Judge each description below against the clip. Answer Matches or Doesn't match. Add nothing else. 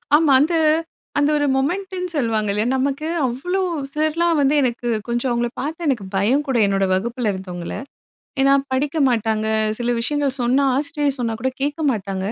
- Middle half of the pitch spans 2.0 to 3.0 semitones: Doesn't match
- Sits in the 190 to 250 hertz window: Doesn't match